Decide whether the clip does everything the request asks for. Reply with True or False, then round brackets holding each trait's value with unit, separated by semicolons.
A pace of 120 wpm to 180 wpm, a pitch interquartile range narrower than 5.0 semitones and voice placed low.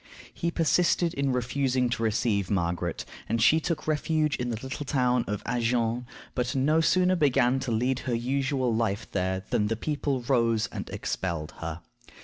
True (165 wpm; 3.8 semitones; 125 Hz)